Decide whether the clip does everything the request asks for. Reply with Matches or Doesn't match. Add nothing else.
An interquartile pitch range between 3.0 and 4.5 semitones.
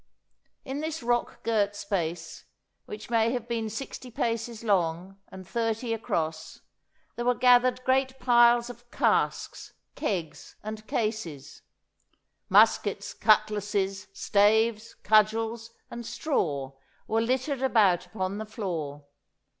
Matches